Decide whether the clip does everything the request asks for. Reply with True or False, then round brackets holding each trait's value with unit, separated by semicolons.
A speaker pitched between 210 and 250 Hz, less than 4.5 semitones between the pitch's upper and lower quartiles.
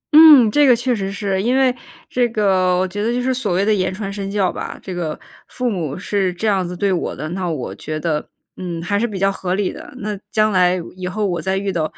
False (195 Hz; 3.0 semitones)